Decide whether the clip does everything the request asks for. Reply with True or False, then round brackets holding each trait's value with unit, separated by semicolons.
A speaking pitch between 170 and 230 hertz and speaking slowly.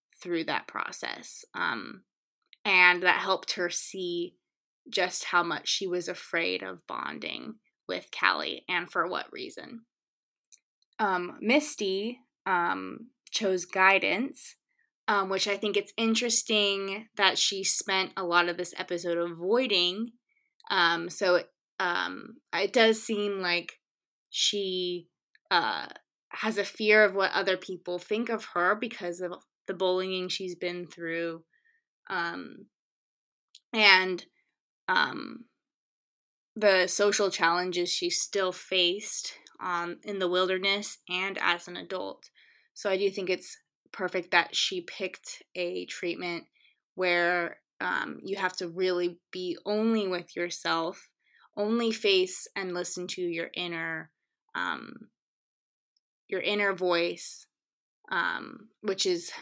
True (190 Hz; 125 wpm)